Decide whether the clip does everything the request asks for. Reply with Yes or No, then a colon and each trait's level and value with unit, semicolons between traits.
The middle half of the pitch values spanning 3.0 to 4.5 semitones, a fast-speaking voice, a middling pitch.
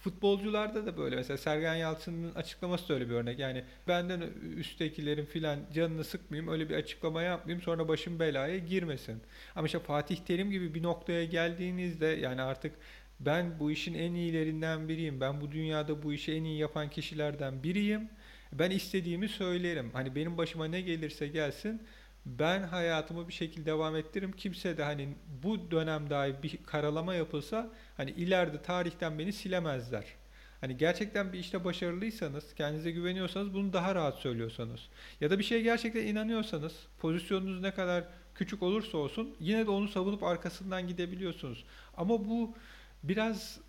Yes: average, 3.5 semitones; fast, 155 wpm; medium, 170 Hz